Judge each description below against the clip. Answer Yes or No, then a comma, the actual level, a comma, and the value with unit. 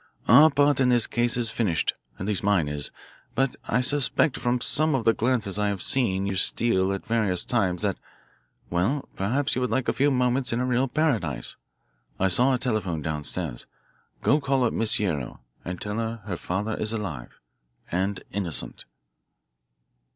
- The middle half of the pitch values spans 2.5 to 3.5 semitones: No, average, 5.1 semitones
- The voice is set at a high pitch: No, low, 110 Hz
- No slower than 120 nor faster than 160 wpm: No, average, 180 wpm